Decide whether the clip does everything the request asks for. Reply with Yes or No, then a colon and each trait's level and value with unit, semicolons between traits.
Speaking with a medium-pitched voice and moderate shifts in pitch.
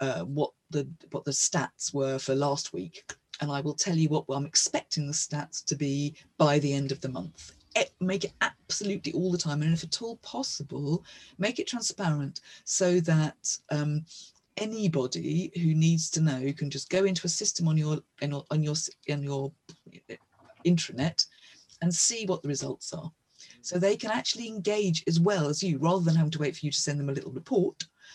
Yes: medium, 155 Hz; average, 3.9 semitones